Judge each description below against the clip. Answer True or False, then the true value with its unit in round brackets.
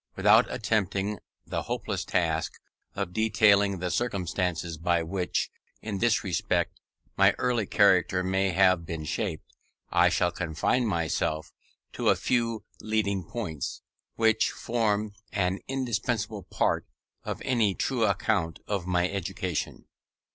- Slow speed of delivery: True (125 wpm)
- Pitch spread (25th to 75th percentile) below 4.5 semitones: True (3.7 semitones)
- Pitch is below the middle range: True (100 Hz)